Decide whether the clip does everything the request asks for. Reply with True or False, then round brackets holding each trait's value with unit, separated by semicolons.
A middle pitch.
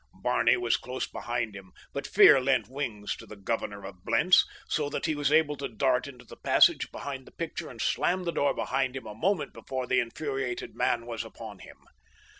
False (130 Hz)